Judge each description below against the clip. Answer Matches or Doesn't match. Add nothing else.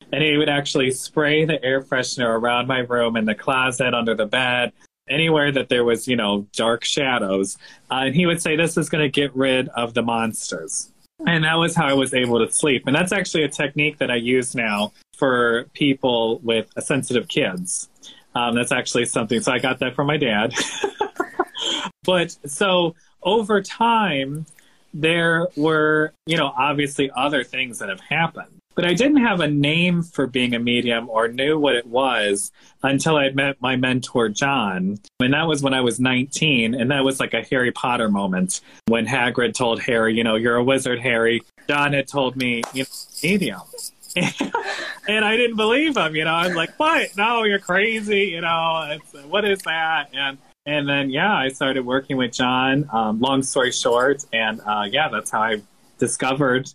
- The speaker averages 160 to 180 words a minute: Doesn't match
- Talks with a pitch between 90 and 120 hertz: Doesn't match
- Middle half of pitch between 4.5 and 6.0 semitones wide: Matches